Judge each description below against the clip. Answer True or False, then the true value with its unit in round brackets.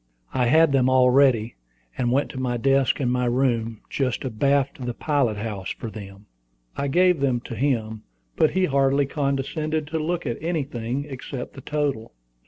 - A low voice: True (130 Hz)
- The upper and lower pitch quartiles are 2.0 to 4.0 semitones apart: True (2.9 semitones)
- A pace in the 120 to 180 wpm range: True (175 wpm)